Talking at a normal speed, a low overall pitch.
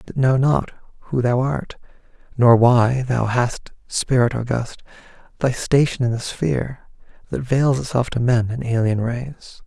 Yes: average, 155 wpm; low, 125 Hz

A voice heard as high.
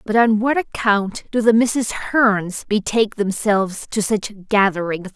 Yes: high, 210 Hz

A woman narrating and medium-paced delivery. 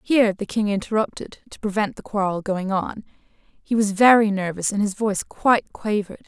Yes: female; average, 180 wpm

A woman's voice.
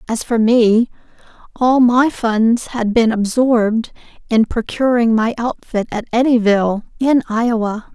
Yes: female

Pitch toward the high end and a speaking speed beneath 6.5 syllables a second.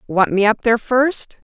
Yes: high, 230 Hz; 4.8 syllables/s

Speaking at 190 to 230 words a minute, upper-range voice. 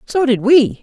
Yes: fast, 220 wpm; very high, 260 Hz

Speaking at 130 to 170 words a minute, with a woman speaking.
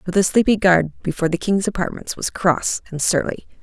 No: average, 200 wpm; female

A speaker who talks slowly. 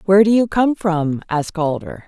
No: average, 200 wpm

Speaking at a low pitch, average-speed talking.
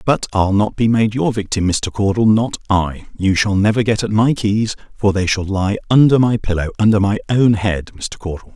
No: low, 105 Hz; fast, 210 wpm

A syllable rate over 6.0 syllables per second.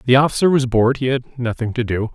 Yes: 6.6 syllables/s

